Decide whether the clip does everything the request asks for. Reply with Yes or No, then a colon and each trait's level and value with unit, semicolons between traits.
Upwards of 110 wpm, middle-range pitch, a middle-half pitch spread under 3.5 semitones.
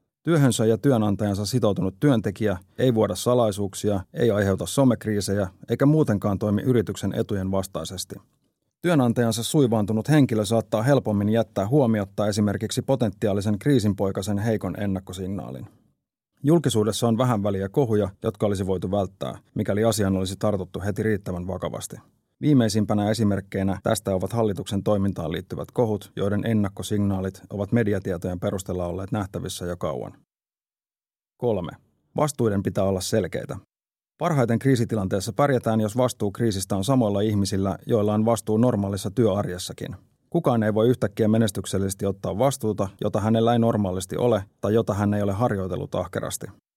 No: average, 130 wpm; low, 105 Hz; average, 2.9 semitones